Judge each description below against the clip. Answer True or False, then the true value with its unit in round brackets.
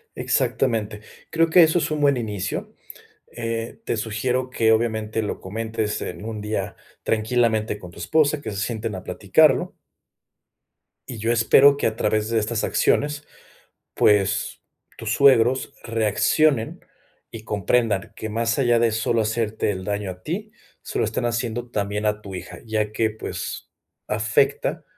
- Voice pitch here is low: True (110 Hz)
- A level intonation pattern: True (2.3 semitones)